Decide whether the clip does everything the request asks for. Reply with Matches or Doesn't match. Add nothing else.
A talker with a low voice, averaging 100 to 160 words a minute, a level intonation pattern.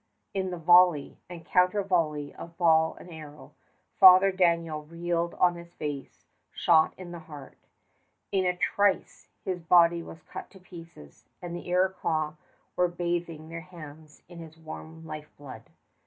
Doesn't match